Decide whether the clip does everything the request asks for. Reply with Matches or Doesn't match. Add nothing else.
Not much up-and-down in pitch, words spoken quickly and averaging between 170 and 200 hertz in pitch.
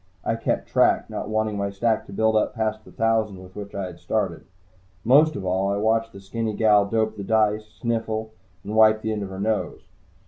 Doesn't match